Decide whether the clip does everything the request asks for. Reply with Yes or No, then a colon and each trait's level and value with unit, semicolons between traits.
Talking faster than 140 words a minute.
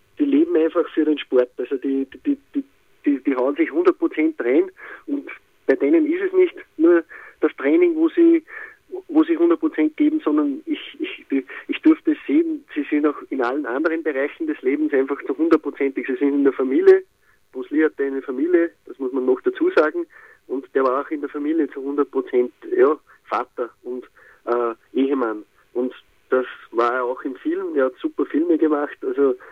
Yes: fast, 190 wpm